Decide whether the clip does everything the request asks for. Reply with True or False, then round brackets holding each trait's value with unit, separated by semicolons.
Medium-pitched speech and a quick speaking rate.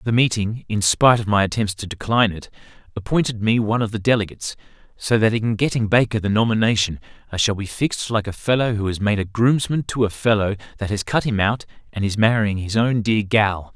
False (110 Hz; 220 wpm)